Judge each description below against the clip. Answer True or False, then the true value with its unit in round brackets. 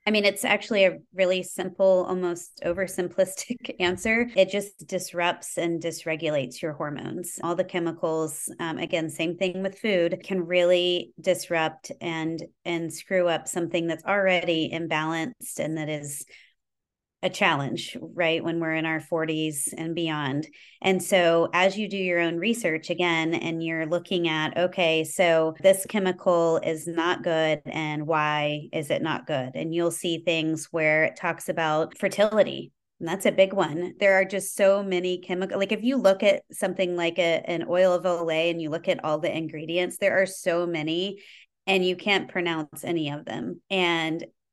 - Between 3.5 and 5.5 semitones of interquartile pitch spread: False (2.7 semitones)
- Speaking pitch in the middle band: True (175 Hz)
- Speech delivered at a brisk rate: False (170 wpm)